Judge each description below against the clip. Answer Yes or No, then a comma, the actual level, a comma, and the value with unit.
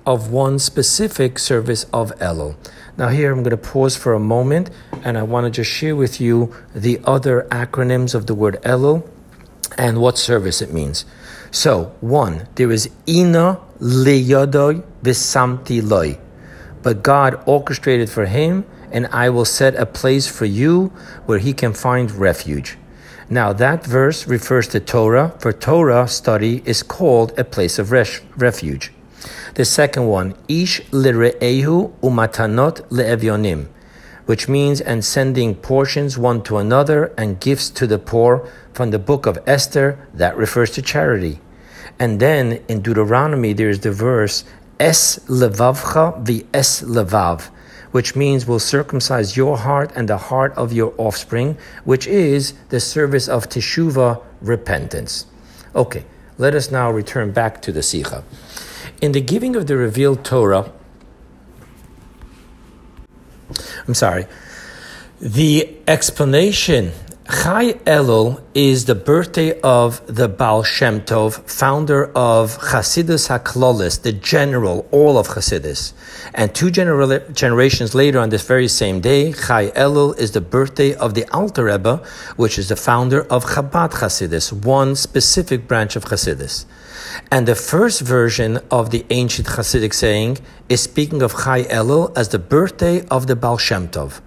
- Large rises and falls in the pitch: No, average, 3.8 semitones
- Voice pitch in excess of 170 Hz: No, low, 125 Hz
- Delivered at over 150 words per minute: No, average, 145 wpm